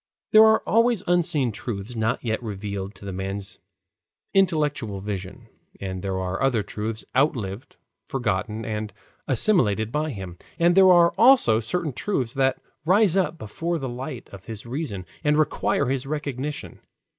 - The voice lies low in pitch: Yes, low, 125 Hz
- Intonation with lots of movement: Yes, wide, 7.4 semitones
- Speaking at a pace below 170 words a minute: Yes, average, 150 wpm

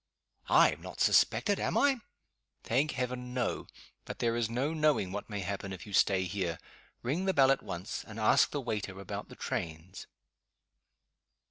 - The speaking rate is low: No, average, 170 wpm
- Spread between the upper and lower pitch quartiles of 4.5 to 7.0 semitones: Yes, wide, 5.5 semitones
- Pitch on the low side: Yes, low, 115 Hz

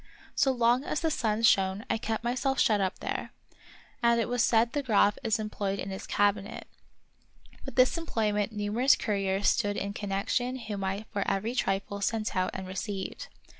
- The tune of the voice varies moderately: Yes, average, 3.1 semitones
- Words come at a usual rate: Yes, average, 180 wpm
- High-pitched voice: Yes, high, 210 Hz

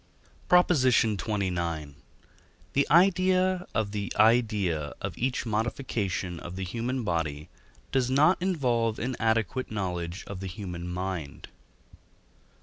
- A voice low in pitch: Yes, low, 110 Hz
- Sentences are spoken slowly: Yes, slow, 115 wpm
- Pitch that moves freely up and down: Yes, wide, 6.4 semitones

